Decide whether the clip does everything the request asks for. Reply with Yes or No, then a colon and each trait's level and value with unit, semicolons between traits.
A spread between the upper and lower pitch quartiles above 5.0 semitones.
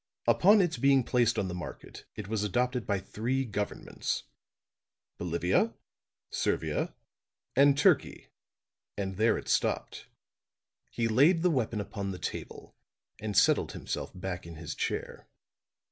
Yes: wide, 5.5 semitones